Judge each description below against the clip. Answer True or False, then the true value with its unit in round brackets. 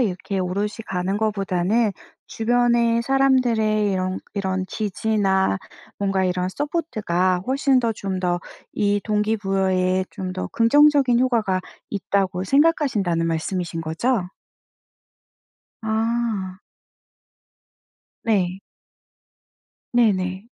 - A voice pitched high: True (200 Hz)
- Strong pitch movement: False (3.9 semitones)